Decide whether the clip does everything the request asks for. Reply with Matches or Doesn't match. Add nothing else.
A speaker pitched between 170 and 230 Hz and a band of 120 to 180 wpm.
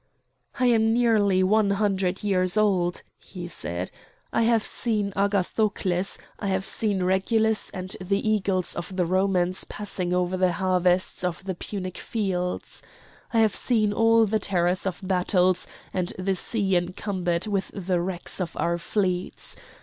Matches